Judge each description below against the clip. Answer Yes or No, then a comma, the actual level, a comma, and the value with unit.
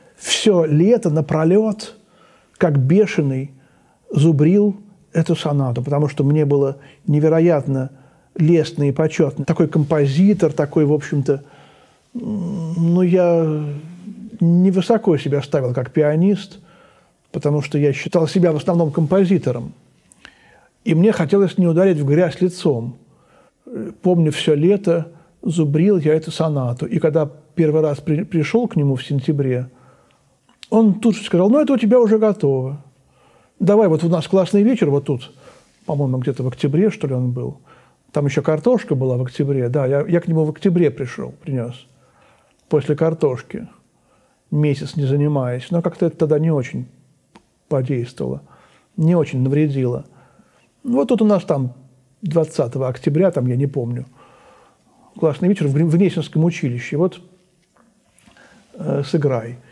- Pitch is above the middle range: No, medium, 160 Hz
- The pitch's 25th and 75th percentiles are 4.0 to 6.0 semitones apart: Yes, average, 4.3 semitones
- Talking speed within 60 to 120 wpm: No, average, 140 wpm